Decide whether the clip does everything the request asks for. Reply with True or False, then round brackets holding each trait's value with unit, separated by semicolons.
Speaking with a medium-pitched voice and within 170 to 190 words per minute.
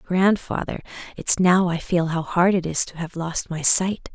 False (175 Hz; 205 wpm)